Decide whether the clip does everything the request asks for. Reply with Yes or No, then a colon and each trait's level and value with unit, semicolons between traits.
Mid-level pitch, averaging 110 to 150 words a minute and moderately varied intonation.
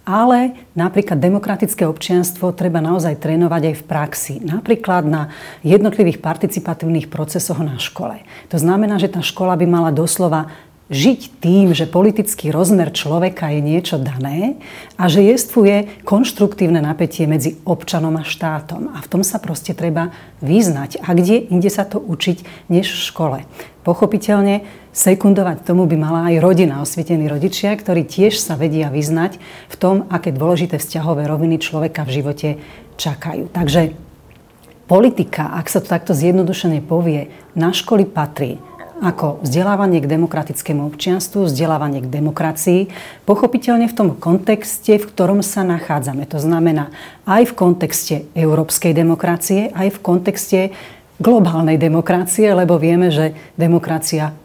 Yes: medium, 175 Hz; average, 140 wpm; average, 3.4 semitones